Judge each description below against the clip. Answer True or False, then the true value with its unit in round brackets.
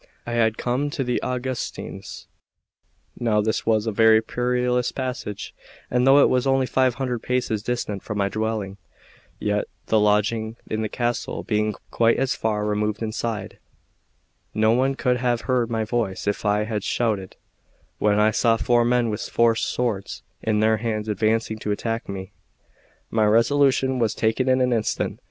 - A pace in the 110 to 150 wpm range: False (170 wpm)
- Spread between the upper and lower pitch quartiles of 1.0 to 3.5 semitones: True (2.6 semitones)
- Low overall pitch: True (115 Hz)